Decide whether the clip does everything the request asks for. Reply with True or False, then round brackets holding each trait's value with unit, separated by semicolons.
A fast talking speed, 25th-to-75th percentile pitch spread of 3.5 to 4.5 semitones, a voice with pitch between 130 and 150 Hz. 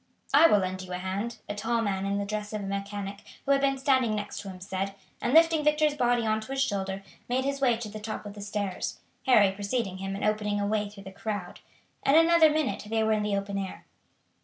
False (245 wpm; 4.0 semitones; 210 Hz)